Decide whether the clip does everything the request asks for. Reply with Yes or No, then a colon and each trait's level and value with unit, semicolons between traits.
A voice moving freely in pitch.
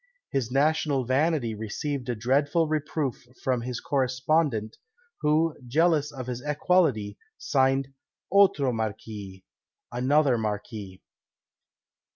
No: average, 4.6 semitones